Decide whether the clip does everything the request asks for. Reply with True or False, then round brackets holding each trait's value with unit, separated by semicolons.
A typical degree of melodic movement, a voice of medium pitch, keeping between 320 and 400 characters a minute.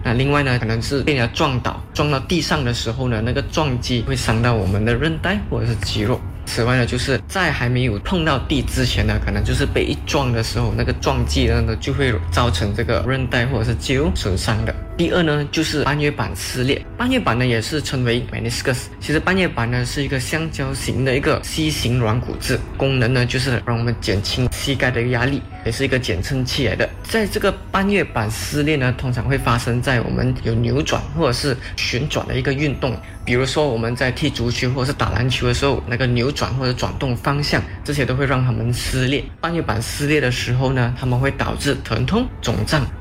False (3.5 semitones; 125 Hz; 335 characters per minute)